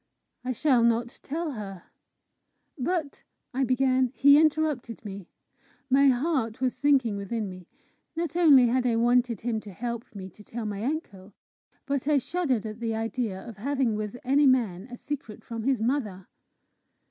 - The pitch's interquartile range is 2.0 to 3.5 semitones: No, average, 4.2 semitones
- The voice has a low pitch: No, high, 245 Hz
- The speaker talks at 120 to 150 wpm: No, average, 160 wpm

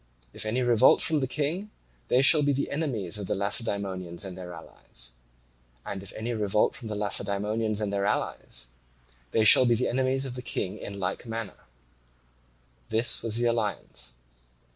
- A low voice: Yes, low, 110 Hz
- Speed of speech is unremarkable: Yes, average, 170 wpm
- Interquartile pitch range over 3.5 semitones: Yes, average, 4.0 semitones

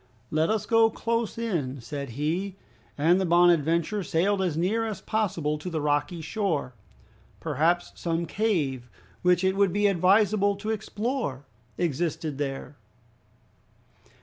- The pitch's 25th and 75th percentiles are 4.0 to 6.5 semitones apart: Yes, average, 5.2 semitones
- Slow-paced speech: Yes, slow, 130 wpm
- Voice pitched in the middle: Yes, medium, 175 Hz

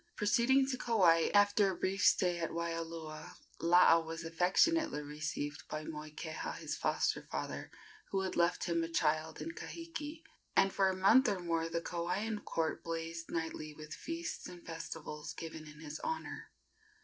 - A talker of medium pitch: Yes, medium, 170 Hz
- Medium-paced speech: Yes, average, 160 wpm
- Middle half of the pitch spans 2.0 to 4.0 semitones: Yes, average, 3.5 semitones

